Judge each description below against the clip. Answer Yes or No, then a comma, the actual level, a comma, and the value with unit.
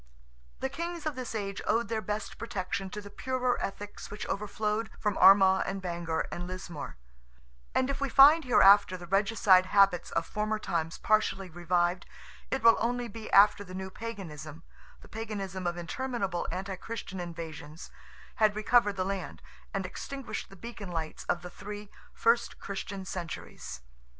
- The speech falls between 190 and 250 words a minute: No, average, 155 wpm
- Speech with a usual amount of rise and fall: Yes, average, 3.6 semitones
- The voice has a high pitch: Yes, high, 195 Hz